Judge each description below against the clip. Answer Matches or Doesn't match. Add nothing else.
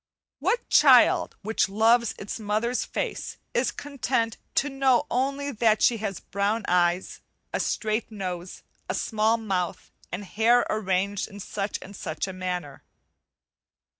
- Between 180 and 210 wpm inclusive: Doesn't match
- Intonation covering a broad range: Doesn't match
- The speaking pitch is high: Matches